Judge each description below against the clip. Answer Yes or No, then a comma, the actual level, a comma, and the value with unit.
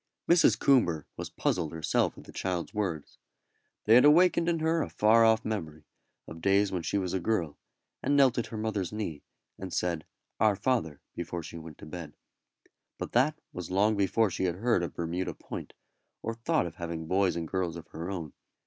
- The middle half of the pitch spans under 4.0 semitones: No, average, 5.0 semitones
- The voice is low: Yes, very low, 95 Hz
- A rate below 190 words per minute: No, average, 195 wpm